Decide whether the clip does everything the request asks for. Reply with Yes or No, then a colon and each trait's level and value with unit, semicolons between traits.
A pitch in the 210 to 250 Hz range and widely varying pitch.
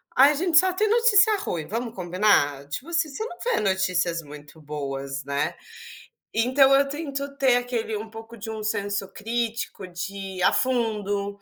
Yes: high, 220 Hz; wide, 7.2 semitones